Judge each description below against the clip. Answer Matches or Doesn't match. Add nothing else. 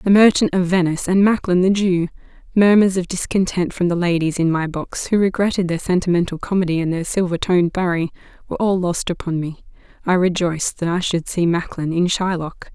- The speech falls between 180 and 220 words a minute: Matches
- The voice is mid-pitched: Matches